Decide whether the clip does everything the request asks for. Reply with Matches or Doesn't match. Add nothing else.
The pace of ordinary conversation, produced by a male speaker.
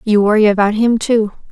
Doesn't match